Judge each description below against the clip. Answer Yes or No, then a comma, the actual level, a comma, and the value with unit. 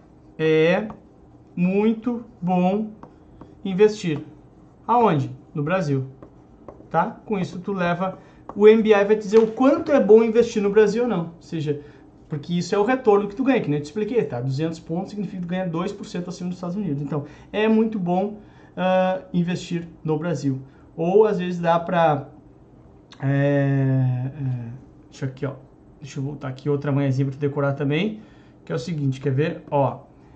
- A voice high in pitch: No, medium, 170 Hz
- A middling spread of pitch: No, wide, 6.2 semitones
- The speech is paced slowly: No, average, 165 wpm